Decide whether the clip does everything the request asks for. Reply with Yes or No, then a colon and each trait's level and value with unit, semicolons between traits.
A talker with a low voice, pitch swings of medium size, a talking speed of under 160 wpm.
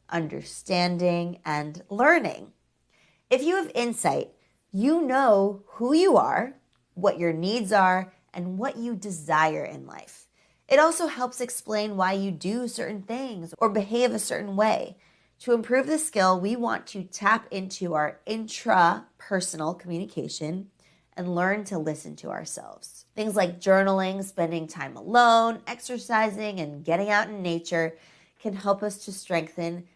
No: high, 200 Hz; average, 4.8 semitones; average, 140 wpm